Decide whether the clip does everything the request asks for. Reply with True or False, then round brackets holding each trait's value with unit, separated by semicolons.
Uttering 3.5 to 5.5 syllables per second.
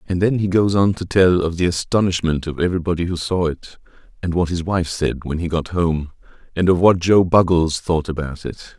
True (5.3 syllables/s)